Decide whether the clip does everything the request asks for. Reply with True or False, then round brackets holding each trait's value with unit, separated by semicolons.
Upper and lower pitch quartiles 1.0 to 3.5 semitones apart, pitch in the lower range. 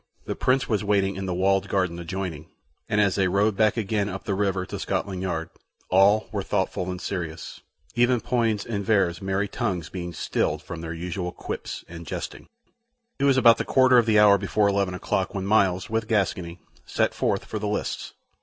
True (2.7 semitones; 95 Hz)